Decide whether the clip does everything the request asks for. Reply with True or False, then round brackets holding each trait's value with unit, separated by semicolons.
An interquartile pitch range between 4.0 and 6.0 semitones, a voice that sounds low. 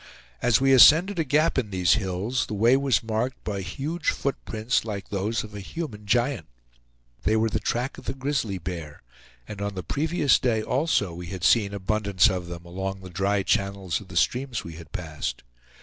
True (5.4 semitones; 105 Hz)